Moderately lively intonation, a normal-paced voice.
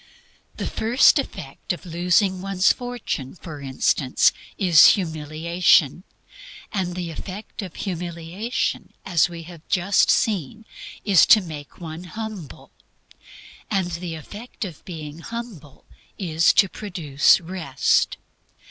No: average, 3.5 semitones; slow, 115 wpm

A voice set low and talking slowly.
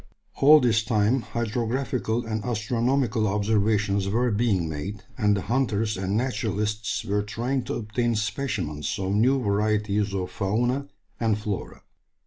Yes: low, 110 Hz; slow, 130 wpm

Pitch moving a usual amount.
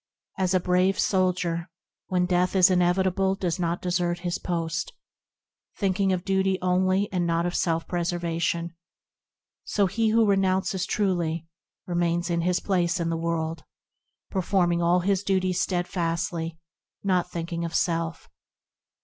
No: narrow, 1.8 semitones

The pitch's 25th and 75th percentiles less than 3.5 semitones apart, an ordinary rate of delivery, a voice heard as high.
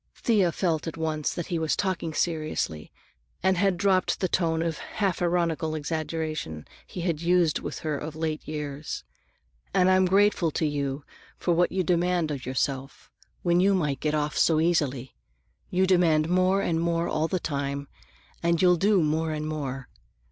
No: average, 2.8 semitones; average, 170 wpm; medium, 165 Hz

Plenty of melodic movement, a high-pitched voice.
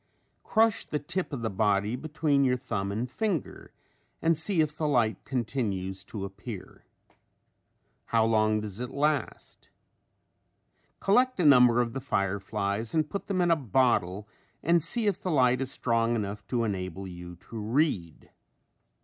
No: wide, 6.7 semitones; low, 120 Hz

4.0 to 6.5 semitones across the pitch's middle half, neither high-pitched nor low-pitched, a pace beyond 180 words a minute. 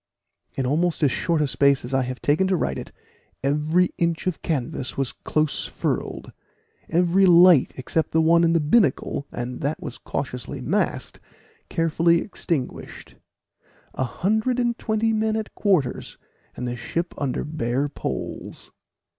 No: average, 4.8 semitones; medium, 160 Hz; average, 150 wpm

